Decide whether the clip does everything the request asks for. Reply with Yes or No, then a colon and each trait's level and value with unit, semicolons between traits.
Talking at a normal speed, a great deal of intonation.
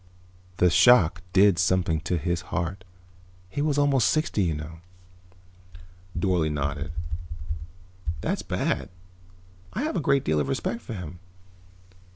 No: slow, 130 wpm; wide, 6.4 semitones